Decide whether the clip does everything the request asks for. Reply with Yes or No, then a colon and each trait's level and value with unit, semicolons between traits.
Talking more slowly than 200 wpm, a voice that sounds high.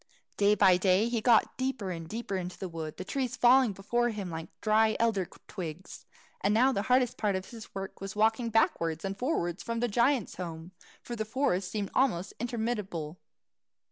Yes: average, 185 wpm; high, 210 Hz